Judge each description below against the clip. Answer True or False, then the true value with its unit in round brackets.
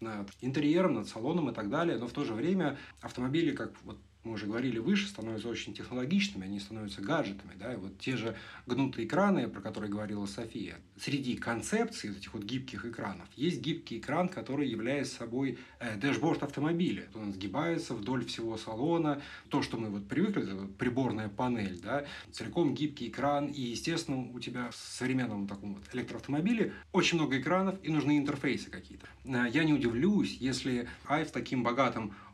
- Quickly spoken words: True (170 wpm)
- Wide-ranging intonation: False (5.0 semitones)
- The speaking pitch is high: False (125 Hz)